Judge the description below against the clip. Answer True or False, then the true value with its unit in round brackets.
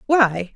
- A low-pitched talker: False (225 Hz)